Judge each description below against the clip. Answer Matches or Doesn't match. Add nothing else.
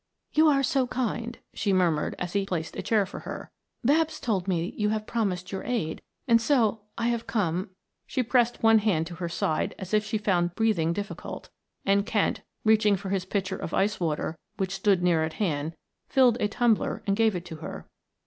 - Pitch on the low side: Doesn't match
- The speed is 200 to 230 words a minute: Matches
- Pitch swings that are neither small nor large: Matches